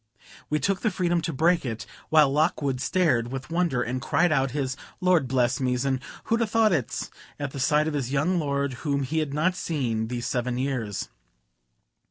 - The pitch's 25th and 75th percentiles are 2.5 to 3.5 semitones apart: No, average, 4.5 semitones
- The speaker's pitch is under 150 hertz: Yes, medium, 140 Hz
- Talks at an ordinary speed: Yes, average, 195 wpm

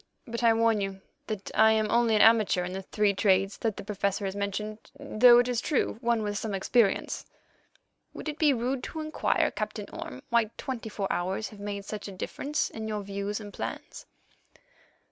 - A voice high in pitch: Yes, high, 215 Hz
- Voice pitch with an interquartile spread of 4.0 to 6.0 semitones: No, average, 2.7 semitones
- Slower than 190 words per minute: No, average, 195 wpm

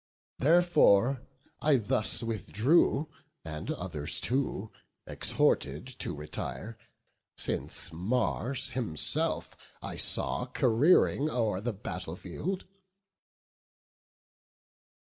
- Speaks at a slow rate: Yes, slow, 80 wpm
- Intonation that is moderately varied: No, wide, 6.8 semitones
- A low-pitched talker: Yes, low, 115 Hz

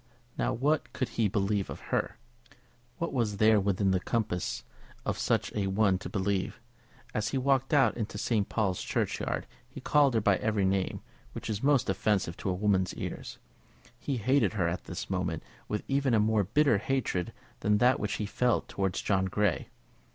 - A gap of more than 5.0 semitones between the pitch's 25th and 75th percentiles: No, average, 4.0 semitones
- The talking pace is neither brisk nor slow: Yes, average, 180 wpm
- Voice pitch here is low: Yes, low, 105 Hz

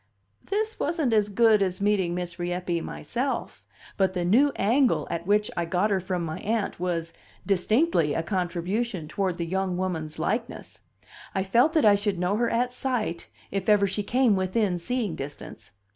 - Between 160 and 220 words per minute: Yes, average, 175 wpm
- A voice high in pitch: Yes, high, 195 Hz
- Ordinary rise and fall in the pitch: Yes, average, 4.5 semitones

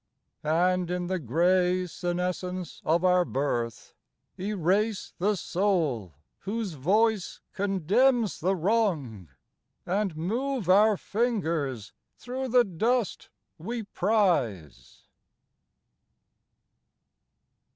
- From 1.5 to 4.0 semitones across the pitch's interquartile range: No, average, 4.5 semitones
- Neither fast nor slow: No, slow, 85 wpm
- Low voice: No, medium, 185 Hz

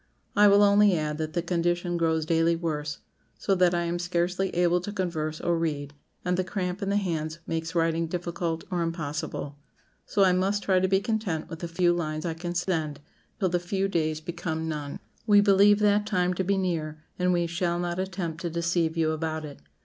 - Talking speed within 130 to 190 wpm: No, fast, 205 wpm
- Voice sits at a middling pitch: Yes, medium, 175 Hz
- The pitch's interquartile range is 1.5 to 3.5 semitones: Yes, narrow, 2.5 semitones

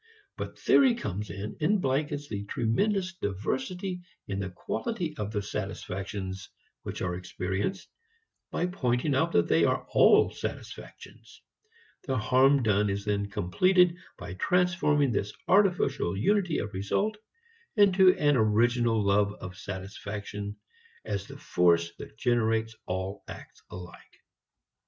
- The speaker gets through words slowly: Yes, slow, 130 wpm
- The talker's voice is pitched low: Yes, low, 115 Hz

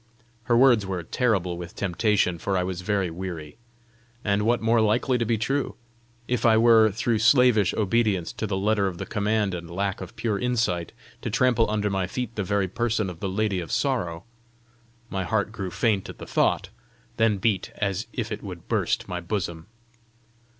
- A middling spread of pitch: Yes, average, 3.5 semitones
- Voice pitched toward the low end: Yes, low, 105 Hz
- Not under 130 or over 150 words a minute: No, average, 185 wpm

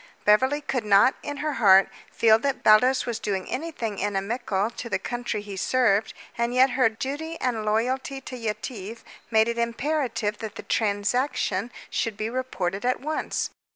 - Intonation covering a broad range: No, average, 3.7 semitones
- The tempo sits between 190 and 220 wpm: No, average, 160 wpm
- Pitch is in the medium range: No, high, 235 Hz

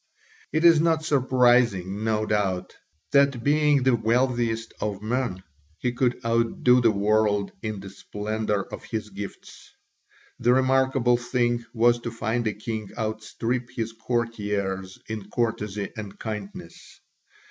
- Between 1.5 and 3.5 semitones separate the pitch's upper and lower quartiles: Yes, average, 2.8 semitones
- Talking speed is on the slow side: Yes, slow, 130 wpm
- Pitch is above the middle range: No, low, 115 Hz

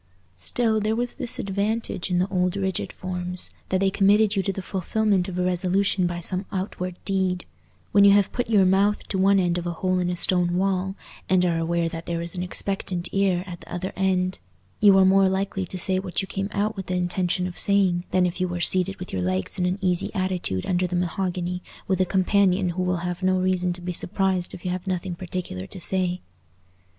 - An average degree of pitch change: No, narrow, 1.5 semitones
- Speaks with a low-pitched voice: No, medium, 185 Hz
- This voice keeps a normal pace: No, fast, 225 wpm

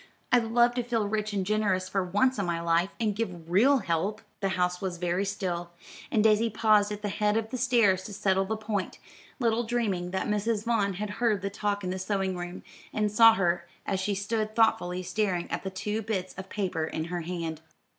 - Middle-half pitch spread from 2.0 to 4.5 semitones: Yes, average, 3.0 semitones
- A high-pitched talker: Yes, high, 200 Hz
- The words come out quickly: Yes, fast, 215 wpm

